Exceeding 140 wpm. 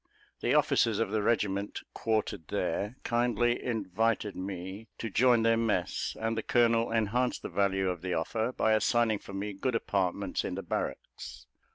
Yes: average, 165 wpm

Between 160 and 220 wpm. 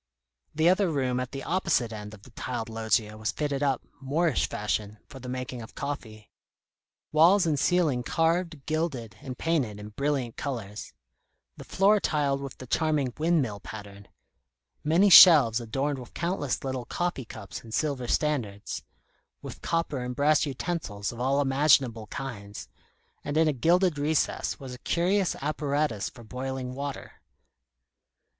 No: average, 150 wpm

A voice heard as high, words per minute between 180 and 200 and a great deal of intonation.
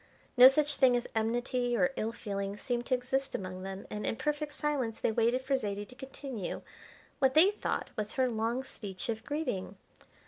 No: high, 245 Hz; average, 185 wpm; average, 3.8 semitones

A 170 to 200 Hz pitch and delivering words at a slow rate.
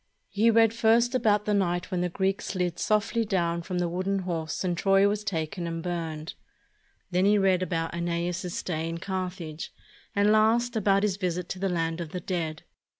No: medium, 185 Hz; average, 195 wpm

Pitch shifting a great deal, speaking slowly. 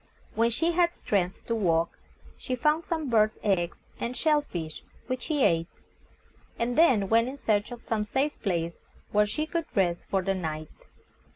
No: wide, 7.2 semitones; average, 175 wpm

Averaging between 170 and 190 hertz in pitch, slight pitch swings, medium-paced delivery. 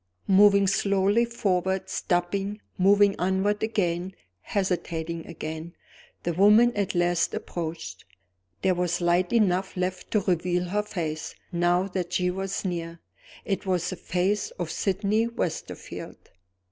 No: medium, 185 Hz; narrow, 2.3 semitones; slow, 125 wpm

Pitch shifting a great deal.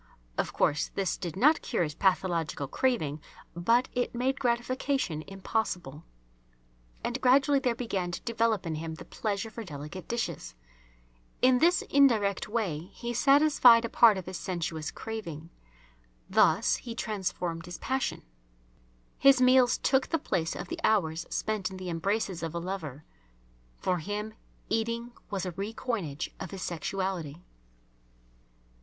Yes: wide, 5.9 semitones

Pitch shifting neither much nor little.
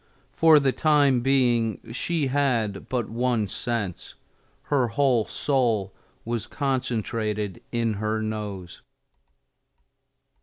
Yes: average, 3.8 semitones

